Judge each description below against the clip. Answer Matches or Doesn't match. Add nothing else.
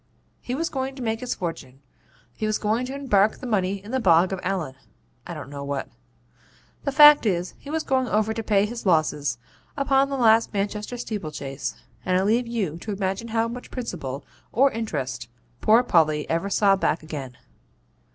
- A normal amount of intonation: Doesn't match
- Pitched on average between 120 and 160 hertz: Doesn't match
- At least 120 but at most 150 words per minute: Doesn't match